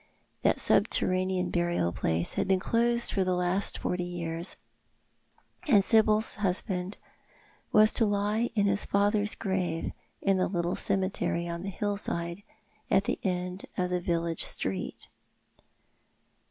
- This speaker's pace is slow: Yes, slow, 130 wpm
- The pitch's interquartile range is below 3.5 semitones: Yes, average, 2.7 semitones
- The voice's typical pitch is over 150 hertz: Yes, medium, 185 Hz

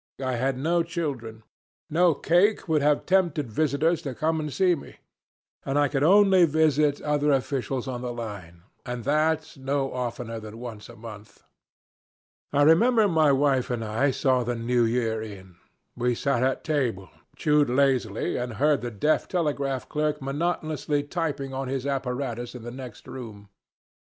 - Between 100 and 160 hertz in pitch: Yes, low, 135 Hz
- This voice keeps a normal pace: Yes, average, 160 wpm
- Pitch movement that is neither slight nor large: Yes, average, 4.0 semitones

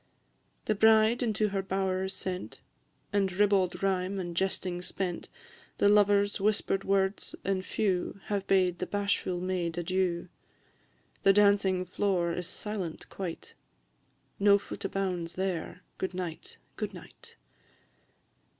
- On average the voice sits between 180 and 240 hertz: Yes, high, 190 Hz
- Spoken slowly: Yes, slow, 125 wpm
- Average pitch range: No, narrow, 1.8 semitones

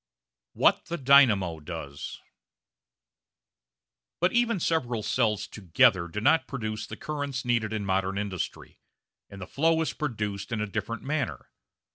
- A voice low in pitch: Yes, low, 110 Hz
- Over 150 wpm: No, slow, 135 wpm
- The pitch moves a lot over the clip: Yes, wide, 6.4 semitones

